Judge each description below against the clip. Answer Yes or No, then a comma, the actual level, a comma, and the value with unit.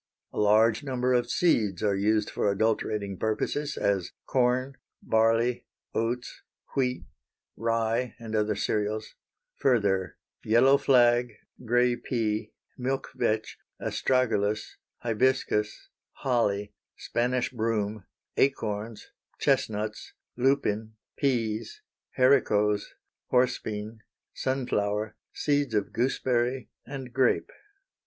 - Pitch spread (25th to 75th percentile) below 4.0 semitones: Yes, average, 3.0 semitones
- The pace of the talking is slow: Yes, slow, 95 wpm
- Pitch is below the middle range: Yes, low, 115 Hz